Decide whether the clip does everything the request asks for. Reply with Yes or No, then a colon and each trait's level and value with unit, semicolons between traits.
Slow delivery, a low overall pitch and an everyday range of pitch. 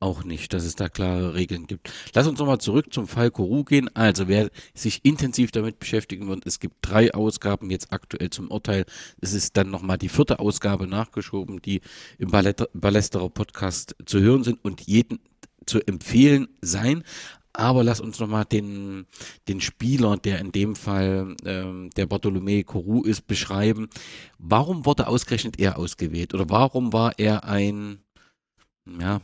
No: average, 160 wpm; low, 105 Hz; average, 3.6 semitones